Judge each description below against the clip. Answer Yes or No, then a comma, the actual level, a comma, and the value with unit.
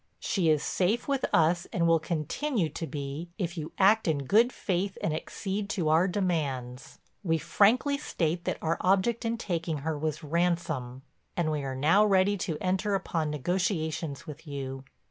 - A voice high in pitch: No, medium, 170 Hz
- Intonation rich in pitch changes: No, average, 3.9 semitones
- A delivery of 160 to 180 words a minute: Yes, average, 170 wpm